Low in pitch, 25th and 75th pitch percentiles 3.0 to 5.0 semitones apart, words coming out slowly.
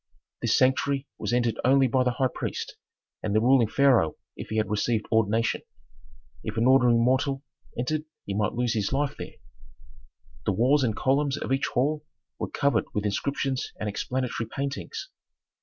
No: low, 125 Hz; average, 3.5 semitones; average, 165 wpm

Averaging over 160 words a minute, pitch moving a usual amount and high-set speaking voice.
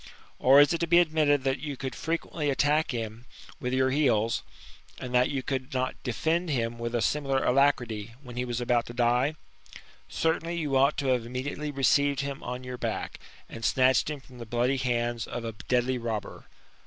No: average, 190 wpm; average, 3.0 semitones; low, 130 Hz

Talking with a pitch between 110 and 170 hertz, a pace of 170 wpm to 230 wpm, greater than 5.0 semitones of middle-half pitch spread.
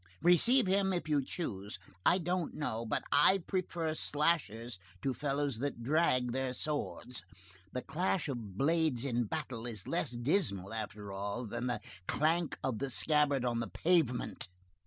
No: low, 135 Hz; average, 155 wpm; wide, 5.5 semitones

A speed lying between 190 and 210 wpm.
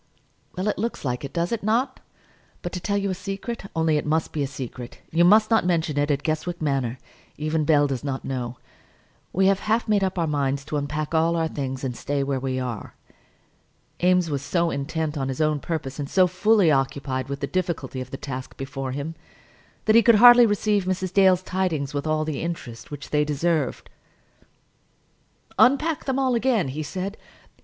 Yes: average, 200 wpm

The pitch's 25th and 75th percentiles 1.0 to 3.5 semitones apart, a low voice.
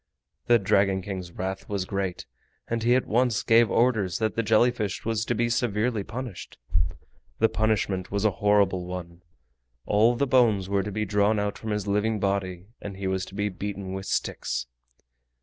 Yes: average, 2.7 semitones; low, 105 Hz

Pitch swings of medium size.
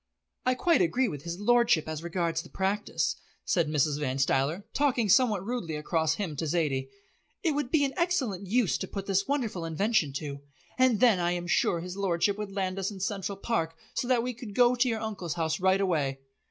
No: wide, 6.3 semitones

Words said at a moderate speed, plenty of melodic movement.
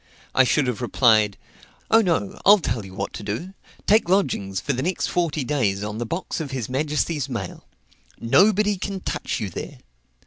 Yes: average, 180 wpm; wide, 8.5 semitones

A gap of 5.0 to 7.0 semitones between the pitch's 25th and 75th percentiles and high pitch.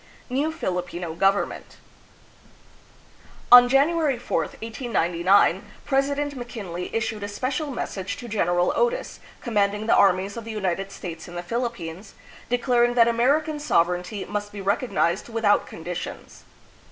Yes: average, 5.3 semitones; high, 215 Hz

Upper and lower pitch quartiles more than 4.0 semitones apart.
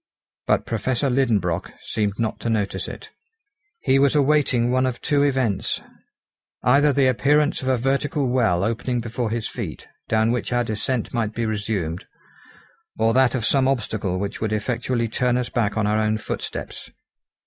No: average, 3.2 semitones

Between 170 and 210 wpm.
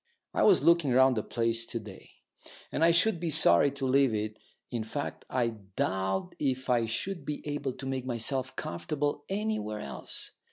Yes: average, 175 wpm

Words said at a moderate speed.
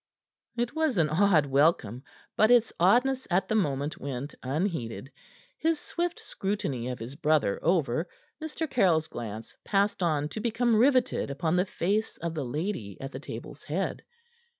Yes: average, 155 wpm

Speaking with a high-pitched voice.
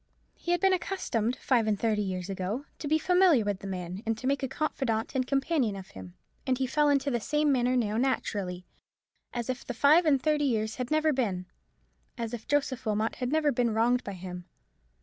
Yes: high, 245 Hz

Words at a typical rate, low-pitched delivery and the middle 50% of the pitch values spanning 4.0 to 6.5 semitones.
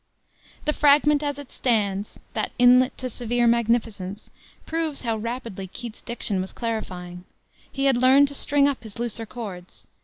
No: average, 155 wpm; high, 235 Hz; average, 4.3 semitones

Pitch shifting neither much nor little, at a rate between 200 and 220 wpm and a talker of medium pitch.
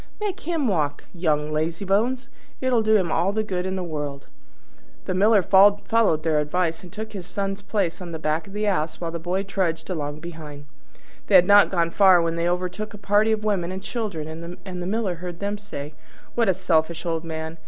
Yes: average, 3.8 semitones; fast, 205 wpm; medium, 180 Hz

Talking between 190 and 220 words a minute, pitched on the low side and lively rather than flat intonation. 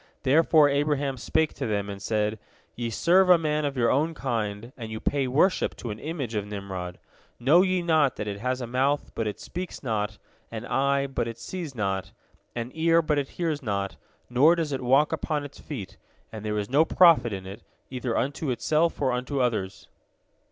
Yes: average, 200 wpm; low, 130 Hz; wide, 5.7 semitones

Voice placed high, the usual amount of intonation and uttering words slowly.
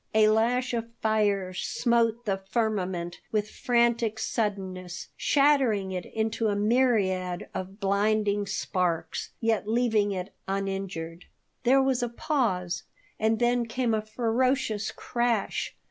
Yes: high, 215 Hz; average, 3.6 semitones; slow, 120 wpm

